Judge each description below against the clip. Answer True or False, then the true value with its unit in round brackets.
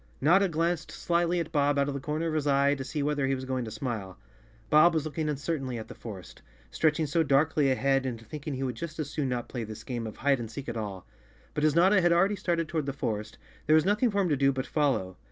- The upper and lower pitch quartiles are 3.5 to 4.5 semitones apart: True (3.8 semitones)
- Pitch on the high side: False (145 Hz)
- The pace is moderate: False (270 wpm)